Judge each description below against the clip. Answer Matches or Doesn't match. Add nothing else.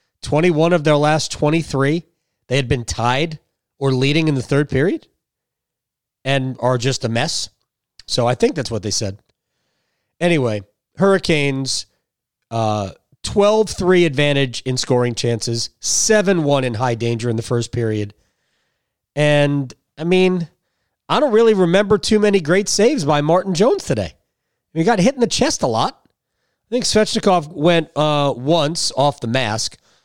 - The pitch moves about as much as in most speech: Doesn't match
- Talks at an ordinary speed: Matches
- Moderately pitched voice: Matches